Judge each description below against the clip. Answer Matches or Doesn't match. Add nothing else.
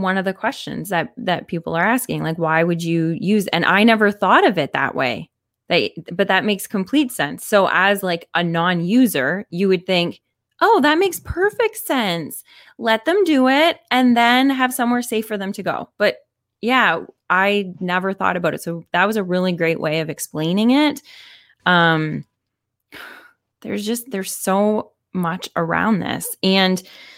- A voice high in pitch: Matches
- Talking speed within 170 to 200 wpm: Matches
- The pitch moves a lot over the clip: Matches